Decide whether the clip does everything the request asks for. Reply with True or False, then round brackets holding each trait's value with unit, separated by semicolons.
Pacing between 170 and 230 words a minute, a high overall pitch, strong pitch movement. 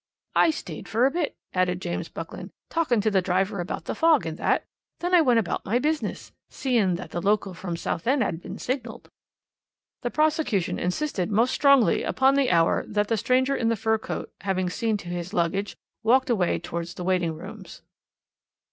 True (185 wpm; 215 Hz; 6.3 semitones)